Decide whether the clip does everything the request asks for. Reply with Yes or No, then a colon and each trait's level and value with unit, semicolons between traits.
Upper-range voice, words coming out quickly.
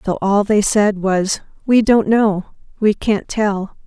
No: high, 205 Hz; average, 155 wpm